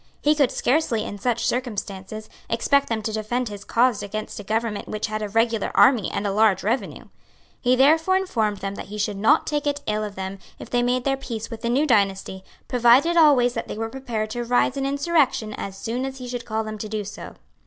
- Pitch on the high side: Yes, high, 230 Hz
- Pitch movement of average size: Yes, average, 3.5 semitones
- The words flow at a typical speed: No, fast, 230 wpm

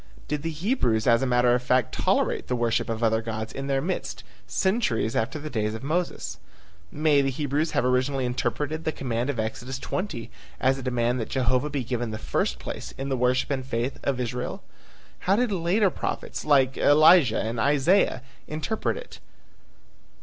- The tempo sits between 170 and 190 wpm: Yes, average, 180 wpm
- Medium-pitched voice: No, low, 130 Hz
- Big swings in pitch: No, average, 4.1 semitones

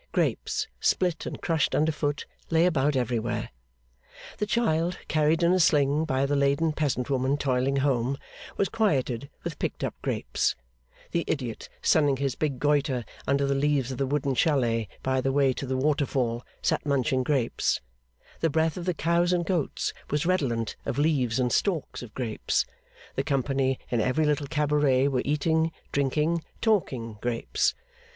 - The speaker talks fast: No, average, 160 wpm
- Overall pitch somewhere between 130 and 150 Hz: Yes, medium, 140 Hz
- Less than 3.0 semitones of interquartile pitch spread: No, average, 3.4 semitones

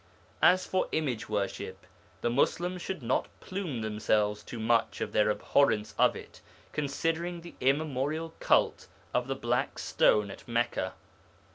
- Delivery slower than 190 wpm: Yes, average, 140 wpm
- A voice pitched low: Yes, low, 130 Hz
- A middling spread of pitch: No, wide, 6.7 semitones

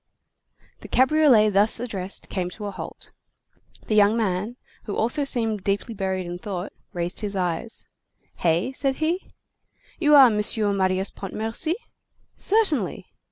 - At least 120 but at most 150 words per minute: Yes, slow, 135 wpm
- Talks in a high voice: Yes, high, 210 Hz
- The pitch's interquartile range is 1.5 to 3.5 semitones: No, average, 5.3 semitones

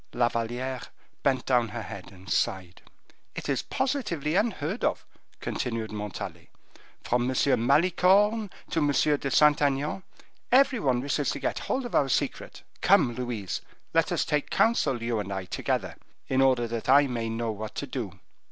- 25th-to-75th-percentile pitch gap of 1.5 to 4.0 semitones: No, average, 4.7 semitones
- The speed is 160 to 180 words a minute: Yes, average, 165 wpm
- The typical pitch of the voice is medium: No, low, 130 Hz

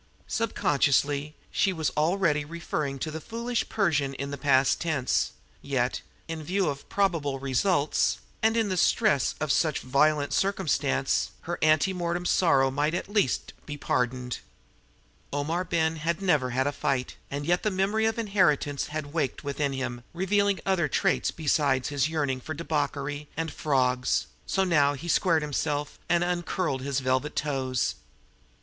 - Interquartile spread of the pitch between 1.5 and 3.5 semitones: No, average, 4.0 semitones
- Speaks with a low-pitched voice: No, medium, 150 Hz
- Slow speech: No, average, 155 wpm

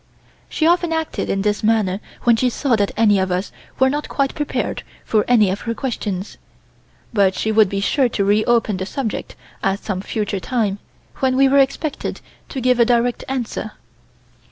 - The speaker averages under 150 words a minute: No, average, 180 wpm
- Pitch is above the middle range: Yes, high, 225 Hz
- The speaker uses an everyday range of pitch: Yes, average, 4.5 semitones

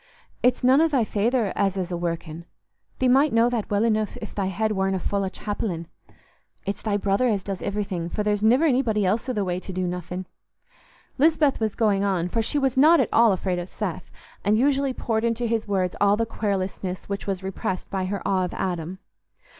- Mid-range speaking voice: No, high, 205 Hz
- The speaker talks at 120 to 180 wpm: No, fast, 205 wpm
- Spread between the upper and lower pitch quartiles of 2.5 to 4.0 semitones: Yes, average, 3.7 semitones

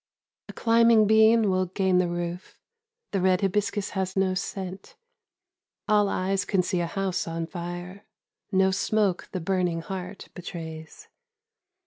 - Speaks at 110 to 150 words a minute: Yes, slow, 135 wpm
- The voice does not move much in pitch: Yes, narrow, 2.1 semitones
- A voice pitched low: No, high, 190 Hz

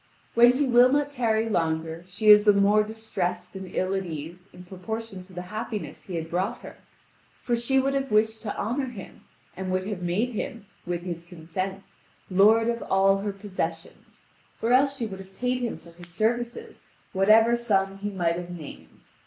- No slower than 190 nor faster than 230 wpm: Yes, average, 195 wpm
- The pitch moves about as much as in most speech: Yes, average, 4.2 semitones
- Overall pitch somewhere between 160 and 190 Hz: No, high, 200 Hz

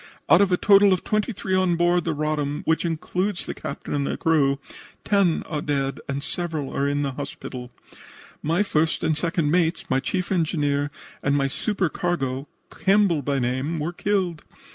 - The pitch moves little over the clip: No, average, 4.0 semitones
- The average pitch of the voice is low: No, medium, 160 Hz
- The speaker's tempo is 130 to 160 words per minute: No, average, 175 wpm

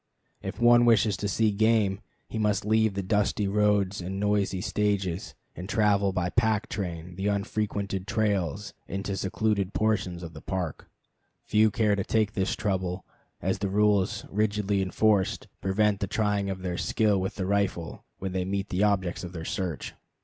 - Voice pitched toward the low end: Yes, low, 100 Hz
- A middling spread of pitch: No, narrow, 2.0 semitones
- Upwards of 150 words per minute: Yes, average, 170 wpm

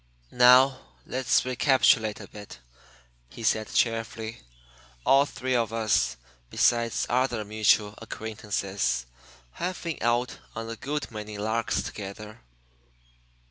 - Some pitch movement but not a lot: Yes, average, 3.0 semitones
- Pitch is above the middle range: No, low, 115 Hz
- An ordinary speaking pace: No, slow, 110 wpm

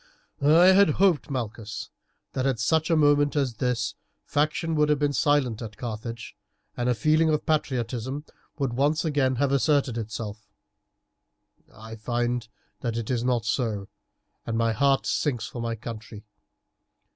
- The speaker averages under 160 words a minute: Yes, average, 150 wpm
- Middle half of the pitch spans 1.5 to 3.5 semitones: No, average, 4.2 semitones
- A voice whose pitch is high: No, low, 125 Hz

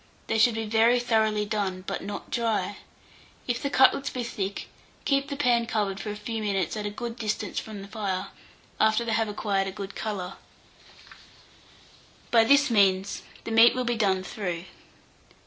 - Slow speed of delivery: No, average, 175 wpm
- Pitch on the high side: Yes, high, 215 Hz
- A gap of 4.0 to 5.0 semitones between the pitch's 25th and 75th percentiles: No, average, 2.8 semitones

